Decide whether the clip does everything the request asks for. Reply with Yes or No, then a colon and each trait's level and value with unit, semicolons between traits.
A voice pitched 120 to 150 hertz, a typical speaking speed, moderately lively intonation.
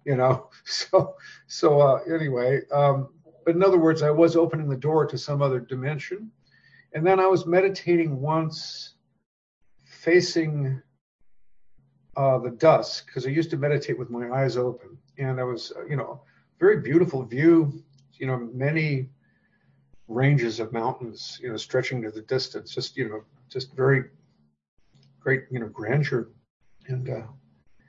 Yes: low, 135 Hz; average, 150 wpm; average, 4.0 semitones